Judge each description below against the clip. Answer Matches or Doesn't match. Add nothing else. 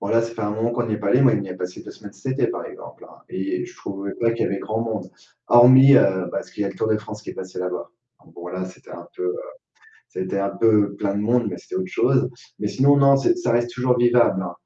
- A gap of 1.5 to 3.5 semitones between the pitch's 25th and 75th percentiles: Doesn't match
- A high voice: Doesn't match